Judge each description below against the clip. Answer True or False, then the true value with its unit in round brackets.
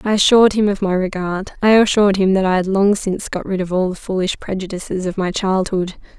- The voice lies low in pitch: False (190 Hz)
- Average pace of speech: False (235 wpm)